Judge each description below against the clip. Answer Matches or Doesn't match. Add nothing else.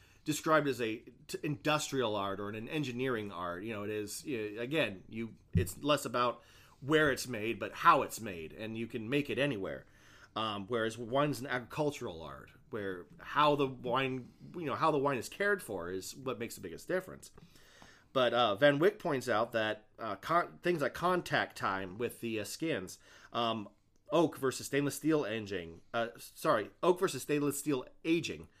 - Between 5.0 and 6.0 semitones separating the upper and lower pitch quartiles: Matches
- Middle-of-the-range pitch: Doesn't match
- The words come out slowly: Doesn't match